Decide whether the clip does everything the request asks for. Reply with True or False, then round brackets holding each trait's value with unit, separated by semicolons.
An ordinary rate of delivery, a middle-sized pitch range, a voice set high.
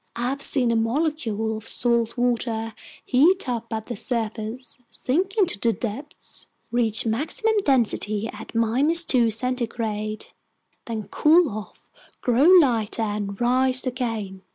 False (130 wpm; 3.2 semitones; 235 Hz)